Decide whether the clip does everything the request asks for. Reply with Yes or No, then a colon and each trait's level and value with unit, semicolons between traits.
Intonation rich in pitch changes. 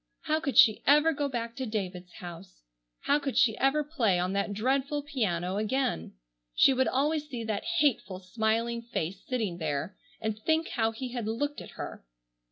Yes: wide, 5.7 semitones